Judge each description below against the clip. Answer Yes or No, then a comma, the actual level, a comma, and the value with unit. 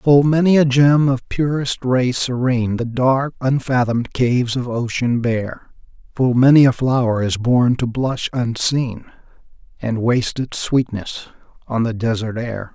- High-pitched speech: No, low, 125 Hz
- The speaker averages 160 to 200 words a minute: No, average, 150 wpm